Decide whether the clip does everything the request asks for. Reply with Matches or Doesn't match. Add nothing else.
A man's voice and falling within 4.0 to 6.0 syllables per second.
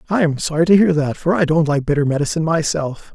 Doesn't match